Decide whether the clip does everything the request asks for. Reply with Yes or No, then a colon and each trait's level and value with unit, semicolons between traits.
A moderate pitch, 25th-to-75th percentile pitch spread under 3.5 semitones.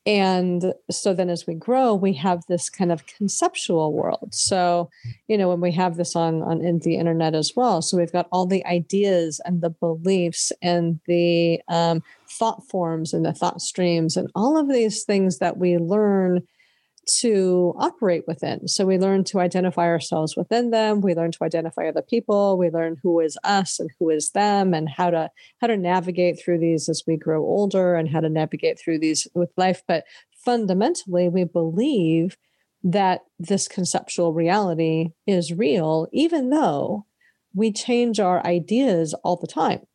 Yes: medium, 180 Hz; average, 2.9 semitones